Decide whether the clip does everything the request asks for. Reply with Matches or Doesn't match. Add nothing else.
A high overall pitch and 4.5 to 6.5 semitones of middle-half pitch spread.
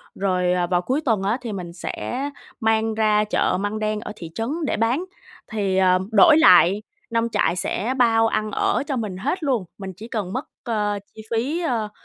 Doesn't match